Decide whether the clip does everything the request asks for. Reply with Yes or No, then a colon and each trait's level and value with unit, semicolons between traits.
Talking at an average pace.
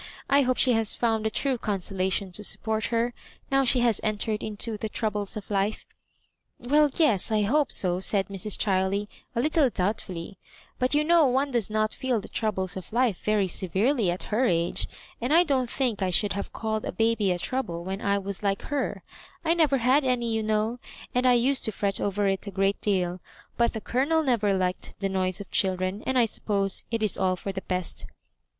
No: fast, 210 wpm